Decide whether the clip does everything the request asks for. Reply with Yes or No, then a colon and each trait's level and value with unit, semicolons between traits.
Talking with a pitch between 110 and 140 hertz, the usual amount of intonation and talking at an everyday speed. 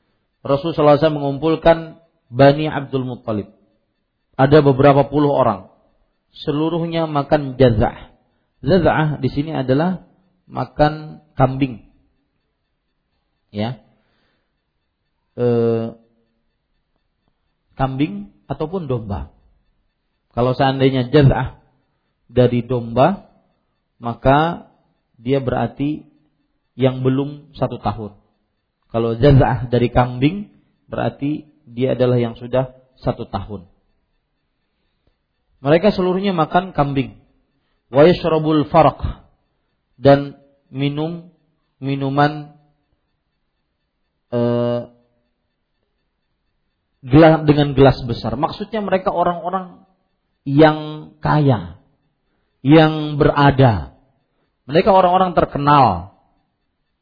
No: low, 135 Hz; average, 4.3 semitones; slow, 70 wpm